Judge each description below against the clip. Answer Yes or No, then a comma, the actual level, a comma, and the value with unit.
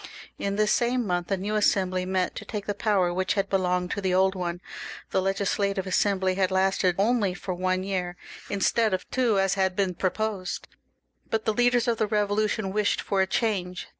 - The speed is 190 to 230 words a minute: Yes, average, 195 wpm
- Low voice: No, high, 195 Hz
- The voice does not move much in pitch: Yes, narrow, 2.2 semitones